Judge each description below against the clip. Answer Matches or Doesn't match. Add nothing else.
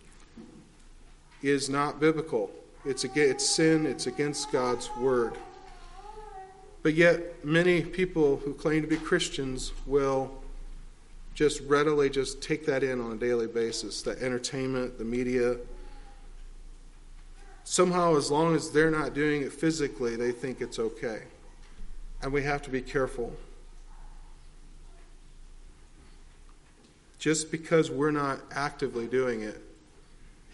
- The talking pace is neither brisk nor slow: Doesn't match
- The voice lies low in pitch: Doesn't match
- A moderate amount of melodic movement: Matches